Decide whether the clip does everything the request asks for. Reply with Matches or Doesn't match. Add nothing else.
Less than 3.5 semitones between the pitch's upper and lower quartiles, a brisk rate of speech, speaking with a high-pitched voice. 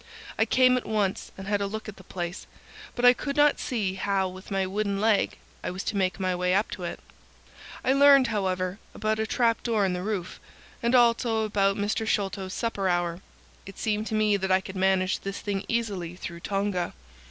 Matches